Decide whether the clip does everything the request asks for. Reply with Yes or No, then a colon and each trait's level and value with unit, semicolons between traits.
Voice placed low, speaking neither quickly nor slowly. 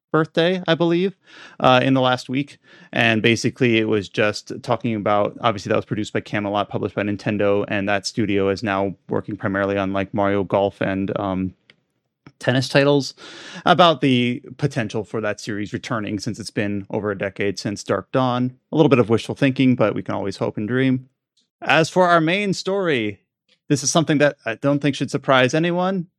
Yes: low, 120 Hz; average, 190 wpm